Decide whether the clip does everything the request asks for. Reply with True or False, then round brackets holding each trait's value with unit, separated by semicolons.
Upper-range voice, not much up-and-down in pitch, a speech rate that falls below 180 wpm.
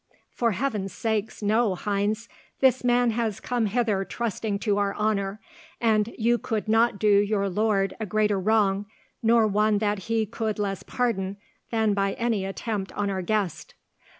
True (215 Hz; 2.2 semitones; 160 wpm)